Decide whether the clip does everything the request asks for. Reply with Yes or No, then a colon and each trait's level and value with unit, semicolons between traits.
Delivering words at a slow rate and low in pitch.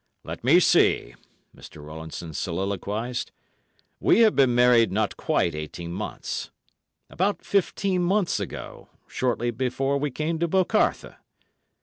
Yes: slow, 115 wpm; low, 125 Hz